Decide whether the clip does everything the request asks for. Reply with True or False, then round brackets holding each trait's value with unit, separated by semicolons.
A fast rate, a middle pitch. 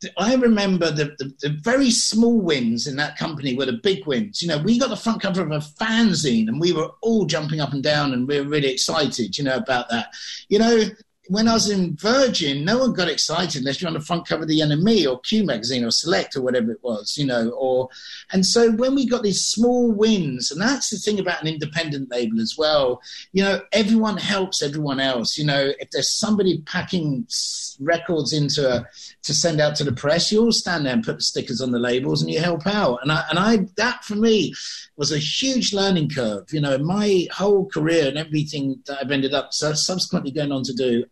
True (230 wpm; 165 Hz)